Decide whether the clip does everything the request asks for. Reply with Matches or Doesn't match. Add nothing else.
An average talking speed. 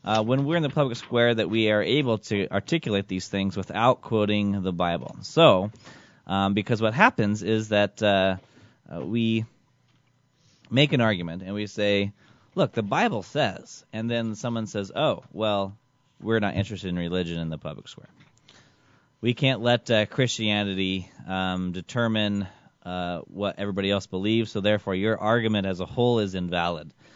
Matches